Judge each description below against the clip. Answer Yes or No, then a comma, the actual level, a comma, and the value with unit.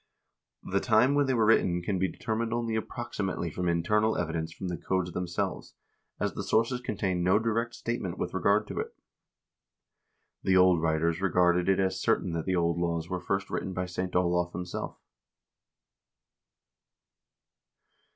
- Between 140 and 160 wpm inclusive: Yes, average, 155 wpm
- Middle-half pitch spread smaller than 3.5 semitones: No, average, 3.8 semitones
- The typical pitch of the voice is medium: No, very low, 95 Hz